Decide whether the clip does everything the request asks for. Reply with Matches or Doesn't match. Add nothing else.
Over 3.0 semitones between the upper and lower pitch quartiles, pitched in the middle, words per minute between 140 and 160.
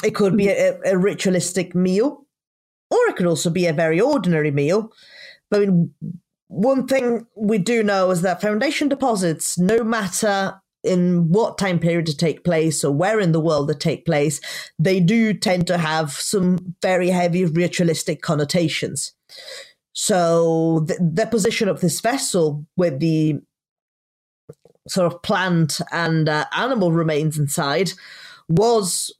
Matches